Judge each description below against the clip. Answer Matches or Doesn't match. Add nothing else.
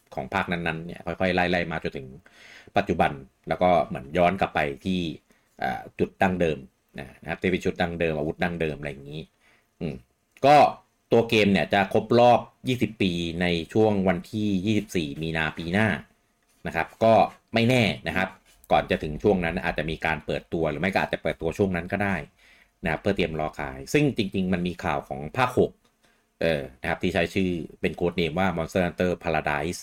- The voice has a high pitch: Doesn't match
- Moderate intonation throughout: Matches